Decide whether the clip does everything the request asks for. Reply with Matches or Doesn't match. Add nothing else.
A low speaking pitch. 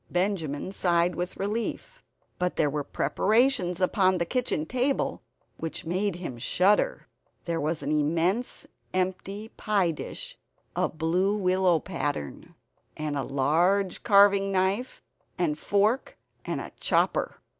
Doesn't match